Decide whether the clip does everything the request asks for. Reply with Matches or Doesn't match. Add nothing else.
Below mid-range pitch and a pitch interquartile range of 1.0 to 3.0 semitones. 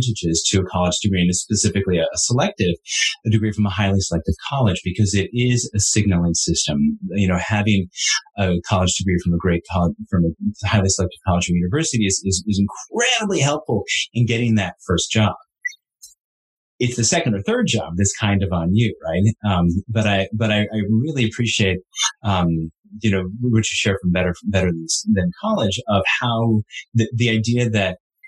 Doesn't match